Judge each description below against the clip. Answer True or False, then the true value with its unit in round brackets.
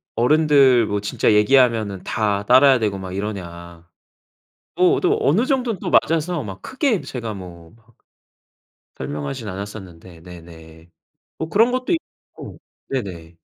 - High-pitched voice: False (105 Hz)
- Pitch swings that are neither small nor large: False (8.1 semitones)